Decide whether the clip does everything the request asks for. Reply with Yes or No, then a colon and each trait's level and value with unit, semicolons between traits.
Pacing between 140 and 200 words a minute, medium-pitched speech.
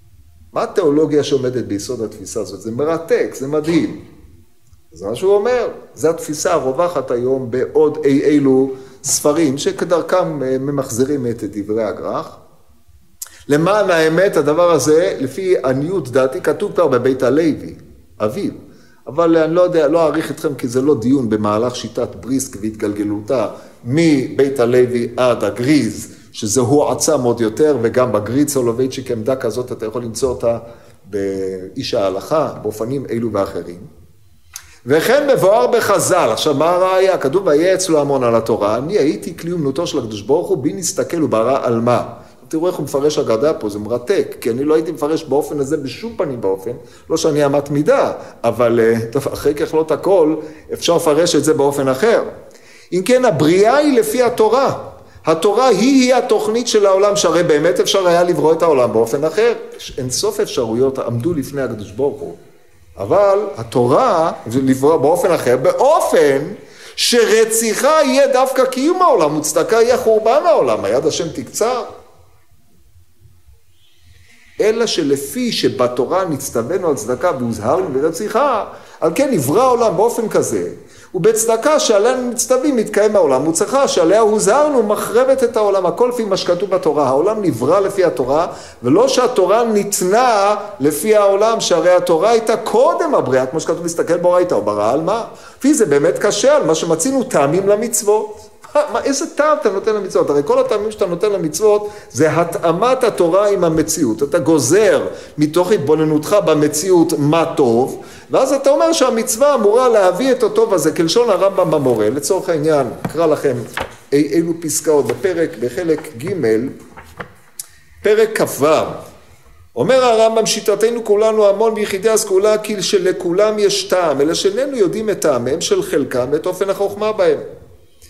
Yes: average, 145 wpm; medium, 170 Hz